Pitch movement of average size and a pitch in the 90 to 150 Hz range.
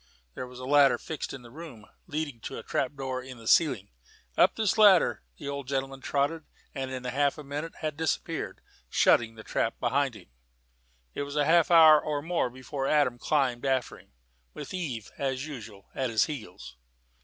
Yes: average, 3.2 semitones; medium, 140 Hz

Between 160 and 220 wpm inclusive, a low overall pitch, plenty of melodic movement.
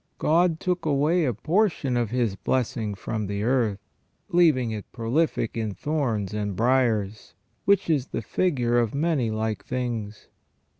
No: average, 145 wpm; low, 120 Hz; wide, 5.9 semitones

